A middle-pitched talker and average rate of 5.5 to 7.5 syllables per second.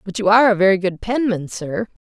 No: high, 200 Hz; 6.0 syllables/s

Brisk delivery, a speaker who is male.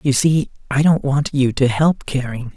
No: average, 190 wpm; male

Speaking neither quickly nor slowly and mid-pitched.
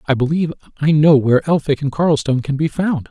No: fast, 215 wpm; medium, 150 Hz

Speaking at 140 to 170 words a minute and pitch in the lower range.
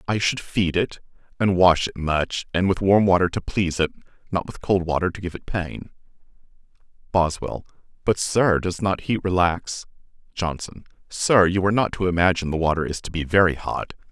No: average, 185 wpm; very low, 90 Hz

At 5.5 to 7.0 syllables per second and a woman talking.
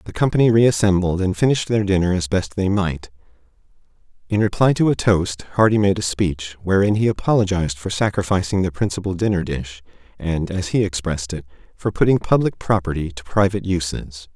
No: 5.7 syllables/s; male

